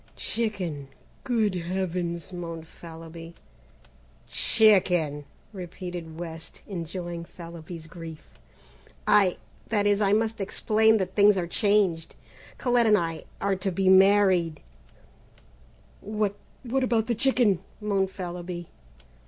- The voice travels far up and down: No, average, 3.8 semitones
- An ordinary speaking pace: No, slow, 110 wpm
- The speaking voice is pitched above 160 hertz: Yes, medium, 185 Hz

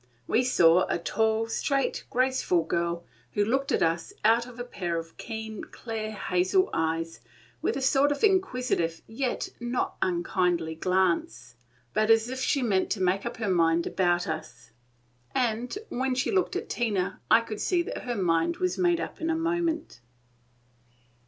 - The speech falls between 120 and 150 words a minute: No, average, 165 wpm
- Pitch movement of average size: No, wide, 6.8 semitones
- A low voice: No, high, 220 Hz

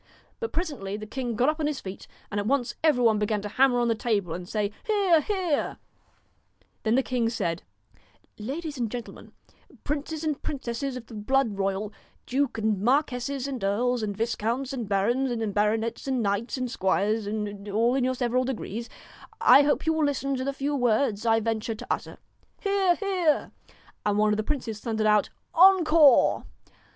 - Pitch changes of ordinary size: Yes, average, 4.7 semitones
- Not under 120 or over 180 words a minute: No, average, 190 wpm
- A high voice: Yes, high, 240 Hz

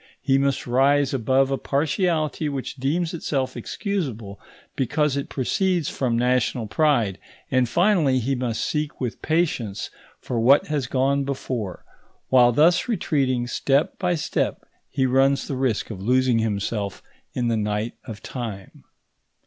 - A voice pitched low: Yes, low, 130 Hz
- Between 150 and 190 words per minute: No, average, 140 wpm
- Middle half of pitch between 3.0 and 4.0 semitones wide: Yes, average, 3.6 semitones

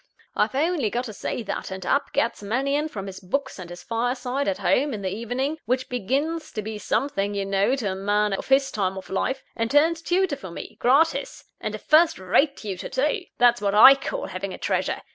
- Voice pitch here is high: Yes, high, 245 Hz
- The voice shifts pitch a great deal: Yes, wide, 5.9 semitones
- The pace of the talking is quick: Yes, fast, 220 wpm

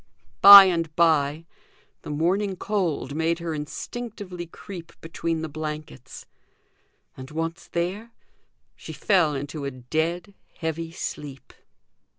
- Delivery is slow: Yes, slow, 115 wpm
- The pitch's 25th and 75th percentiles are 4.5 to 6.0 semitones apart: No, average, 2.9 semitones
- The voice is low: No, medium, 165 Hz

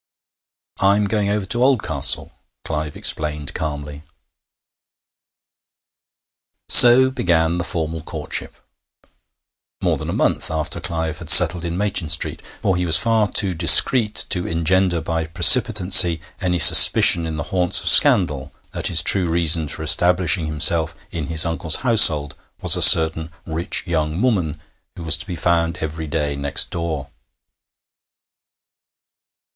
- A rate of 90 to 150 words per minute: Yes, average, 140 wpm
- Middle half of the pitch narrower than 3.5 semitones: Yes, average, 2.8 semitones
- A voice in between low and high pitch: No, very low, 85 Hz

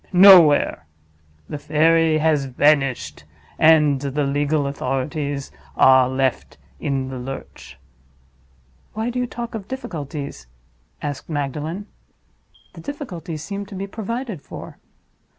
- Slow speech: Yes, slow, 115 wpm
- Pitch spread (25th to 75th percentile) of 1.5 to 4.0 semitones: No, average, 5.3 semitones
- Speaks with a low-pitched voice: No, medium, 150 Hz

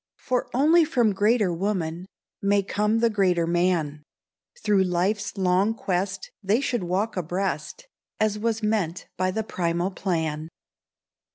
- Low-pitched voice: No, high, 195 Hz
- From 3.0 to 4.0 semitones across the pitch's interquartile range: Yes, average, 3.4 semitones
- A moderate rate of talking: No, slow, 130 wpm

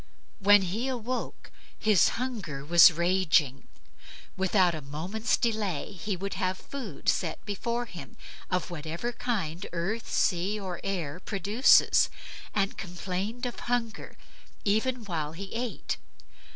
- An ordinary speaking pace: No, slow, 125 wpm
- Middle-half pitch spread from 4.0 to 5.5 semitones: Yes, average, 4.5 semitones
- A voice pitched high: Yes, high, 195 Hz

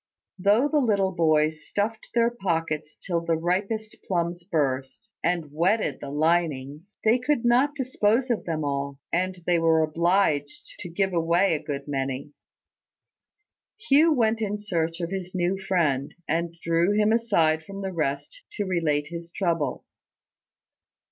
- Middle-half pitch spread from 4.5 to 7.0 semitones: Yes, average, 4.8 semitones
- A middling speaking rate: Yes, average, 150 wpm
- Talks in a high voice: No, medium, 175 Hz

